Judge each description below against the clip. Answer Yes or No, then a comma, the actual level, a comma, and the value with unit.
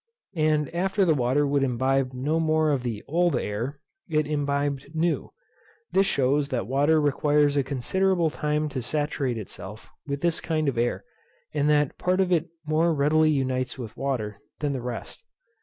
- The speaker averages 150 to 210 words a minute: Yes, average, 170 wpm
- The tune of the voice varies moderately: Yes, average, 3.1 semitones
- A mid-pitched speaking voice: Yes, medium, 145 Hz